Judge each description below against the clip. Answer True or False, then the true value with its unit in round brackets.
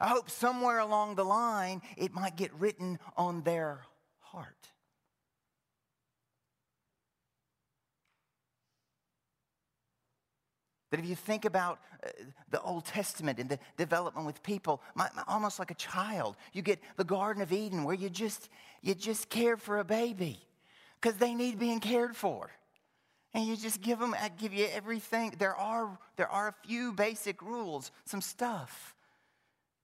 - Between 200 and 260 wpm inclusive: False (145 wpm)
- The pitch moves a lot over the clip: False (4.3 semitones)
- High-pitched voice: True (200 Hz)